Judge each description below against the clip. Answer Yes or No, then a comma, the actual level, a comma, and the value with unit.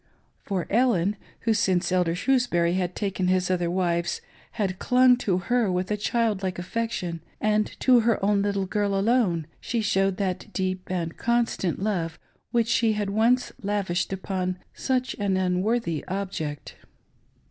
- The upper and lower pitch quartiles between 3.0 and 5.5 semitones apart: Yes, average, 3.6 semitones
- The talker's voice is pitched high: Yes, high, 195 Hz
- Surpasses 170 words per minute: No, average, 150 wpm